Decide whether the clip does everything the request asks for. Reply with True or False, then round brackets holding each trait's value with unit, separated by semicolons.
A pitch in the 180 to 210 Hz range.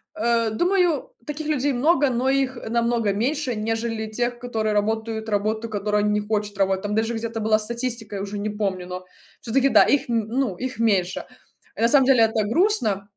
False (225 Hz)